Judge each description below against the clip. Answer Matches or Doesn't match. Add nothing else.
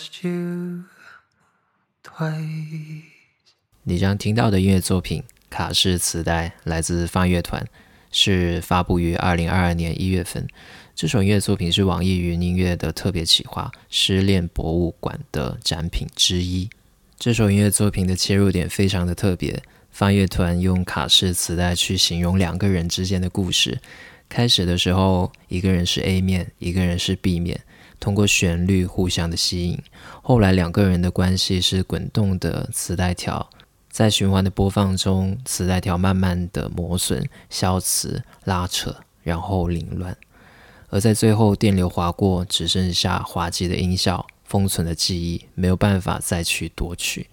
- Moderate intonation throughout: Doesn't match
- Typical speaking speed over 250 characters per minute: Doesn't match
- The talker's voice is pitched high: Doesn't match